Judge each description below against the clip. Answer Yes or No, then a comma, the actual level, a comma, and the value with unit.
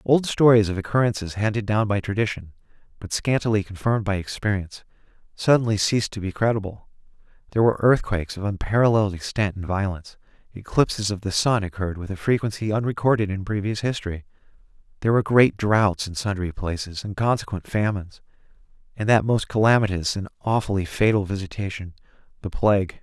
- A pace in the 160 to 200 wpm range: No, average, 150 wpm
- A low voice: Yes, low, 105 Hz